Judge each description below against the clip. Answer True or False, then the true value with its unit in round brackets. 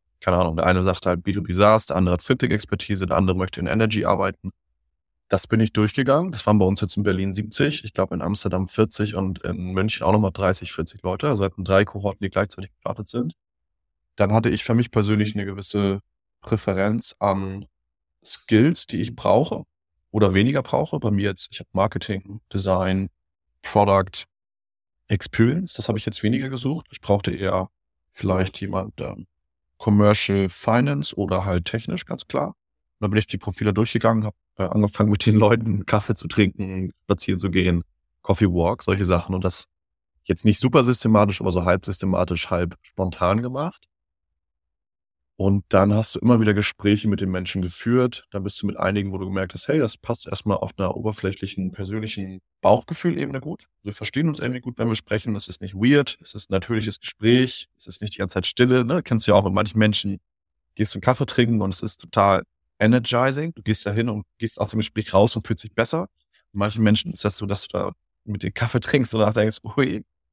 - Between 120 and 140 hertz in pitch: False (100 Hz)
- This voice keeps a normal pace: False (200 wpm)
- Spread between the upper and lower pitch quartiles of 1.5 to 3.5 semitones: True (2.9 semitones)